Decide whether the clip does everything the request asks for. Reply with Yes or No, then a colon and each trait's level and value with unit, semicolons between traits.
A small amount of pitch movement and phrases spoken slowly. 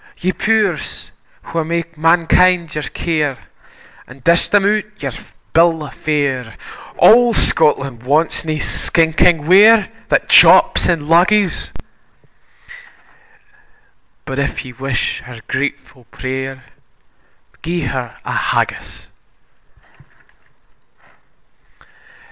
No: average, 4.5 semitones; slow, 95 wpm